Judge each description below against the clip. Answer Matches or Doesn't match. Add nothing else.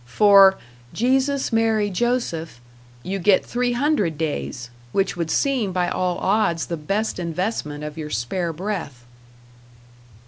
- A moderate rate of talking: Doesn't match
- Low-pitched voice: Doesn't match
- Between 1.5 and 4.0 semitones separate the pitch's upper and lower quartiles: Doesn't match